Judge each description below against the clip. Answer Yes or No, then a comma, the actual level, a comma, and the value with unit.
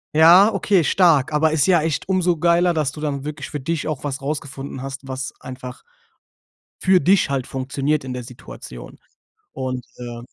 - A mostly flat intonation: No, average, 4.0 semitones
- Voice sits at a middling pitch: Yes, medium, 145 Hz